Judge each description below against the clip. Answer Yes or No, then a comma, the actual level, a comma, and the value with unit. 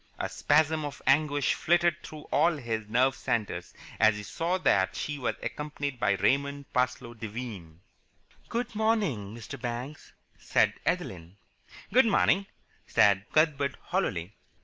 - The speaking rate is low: Yes, slow, 130 wpm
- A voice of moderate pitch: No, low, 130 Hz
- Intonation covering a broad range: Yes, wide, 6.5 semitones